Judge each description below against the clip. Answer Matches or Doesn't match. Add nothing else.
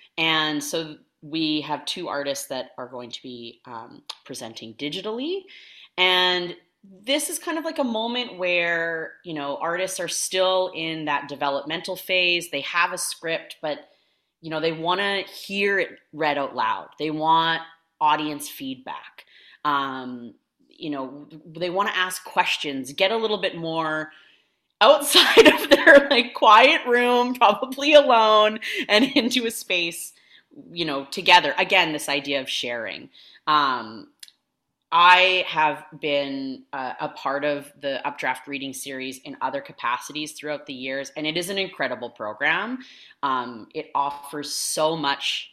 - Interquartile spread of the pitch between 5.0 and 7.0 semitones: Matches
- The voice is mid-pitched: Matches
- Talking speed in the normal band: Matches